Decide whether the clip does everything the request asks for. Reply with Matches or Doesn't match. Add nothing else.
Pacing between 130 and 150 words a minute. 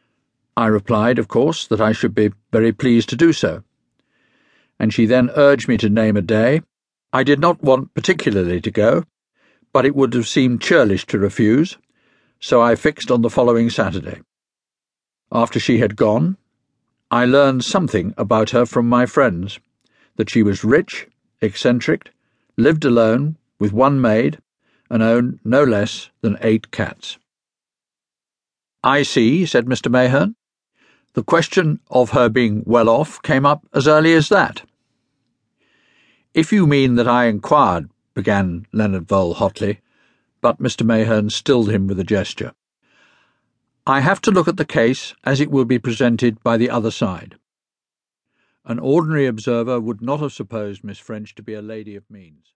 Doesn't match